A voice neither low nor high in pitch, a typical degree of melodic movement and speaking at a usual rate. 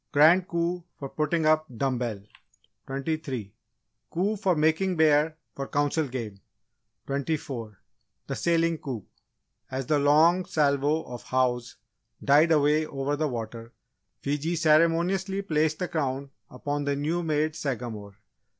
No: medium, 150 Hz; average, 3.3 semitones; slow, 130 wpm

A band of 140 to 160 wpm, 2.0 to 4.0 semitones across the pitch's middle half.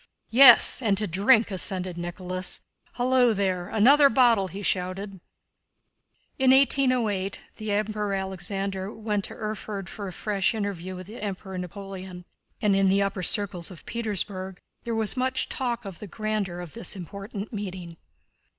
Yes: average, 150 wpm; average, 2.8 semitones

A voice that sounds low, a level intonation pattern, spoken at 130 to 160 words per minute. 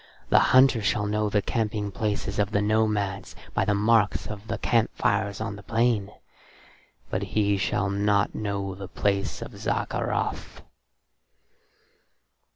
Yes: low, 105 Hz; narrow, 1.4 semitones; average, 140 wpm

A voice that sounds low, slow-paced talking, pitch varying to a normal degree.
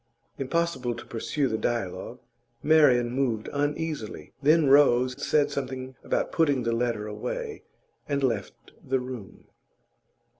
Yes: low, 130 Hz; slow, 120 wpm; average, 3.6 semitones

